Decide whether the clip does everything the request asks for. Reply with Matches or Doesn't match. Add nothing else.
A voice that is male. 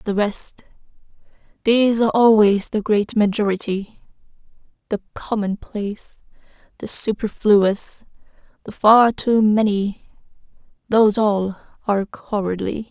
Doesn't match